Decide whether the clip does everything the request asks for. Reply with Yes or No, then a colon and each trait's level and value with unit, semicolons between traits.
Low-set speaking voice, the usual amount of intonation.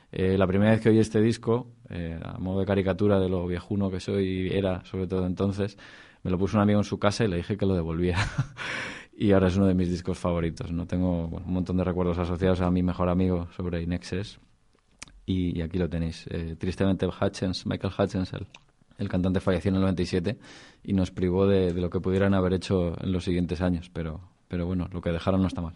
No: very low, 95 Hz; narrow, 1.8 semitones